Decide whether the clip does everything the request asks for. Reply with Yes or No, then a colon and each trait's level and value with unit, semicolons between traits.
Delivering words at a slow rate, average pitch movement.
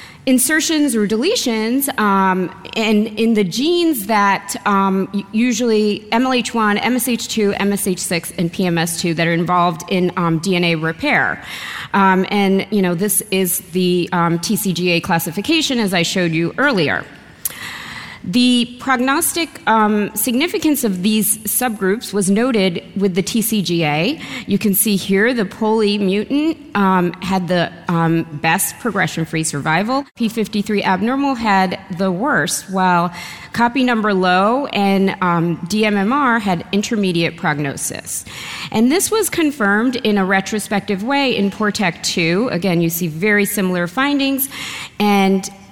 Yes: slow, 125 wpm; average, 4.1 semitones